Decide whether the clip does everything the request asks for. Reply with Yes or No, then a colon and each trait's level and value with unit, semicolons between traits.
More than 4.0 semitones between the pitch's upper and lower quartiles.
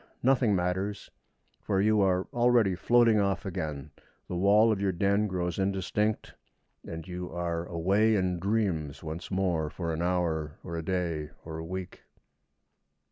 No: average, 3.3 semitones